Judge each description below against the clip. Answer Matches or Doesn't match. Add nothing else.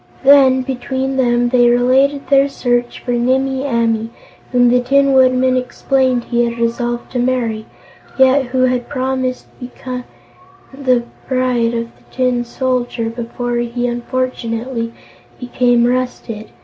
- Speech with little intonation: Matches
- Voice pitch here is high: Matches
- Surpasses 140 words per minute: Doesn't match